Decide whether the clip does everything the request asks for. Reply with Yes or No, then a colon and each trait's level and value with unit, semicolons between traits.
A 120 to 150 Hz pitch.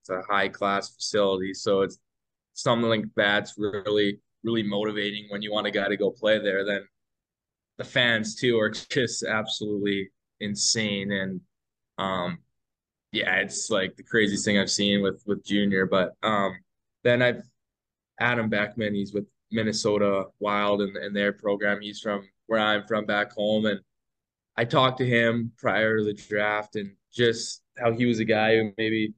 No: low, 105 Hz